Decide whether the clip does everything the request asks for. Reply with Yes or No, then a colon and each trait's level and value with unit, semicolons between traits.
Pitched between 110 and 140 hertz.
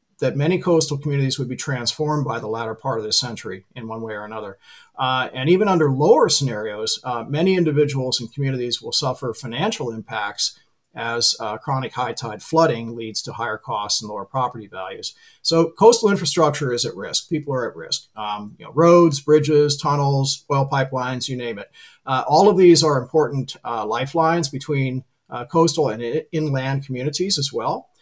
Yes: low, 135 Hz